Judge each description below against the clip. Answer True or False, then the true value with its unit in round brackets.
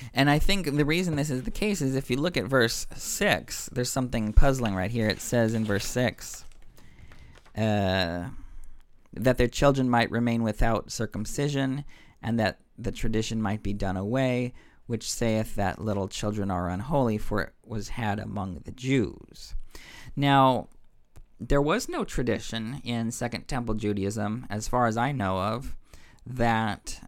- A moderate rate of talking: True (160 wpm)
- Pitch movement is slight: False (3.8 semitones)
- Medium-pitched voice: False (115 Hz)